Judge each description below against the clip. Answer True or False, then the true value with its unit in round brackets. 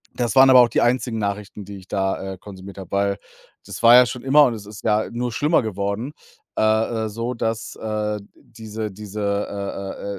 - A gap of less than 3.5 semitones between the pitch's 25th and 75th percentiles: True (2.9 semitones)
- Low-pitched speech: True (105 Hz)